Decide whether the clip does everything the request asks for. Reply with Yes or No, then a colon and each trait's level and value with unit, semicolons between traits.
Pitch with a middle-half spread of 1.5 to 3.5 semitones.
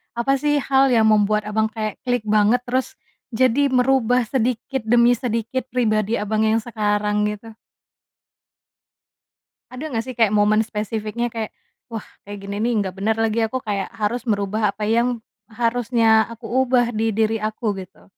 Yes: narrow, 2.5 semitones